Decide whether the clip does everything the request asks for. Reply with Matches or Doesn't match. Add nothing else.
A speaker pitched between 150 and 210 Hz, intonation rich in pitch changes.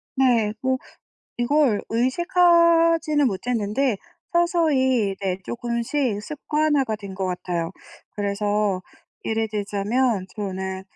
Doesn't match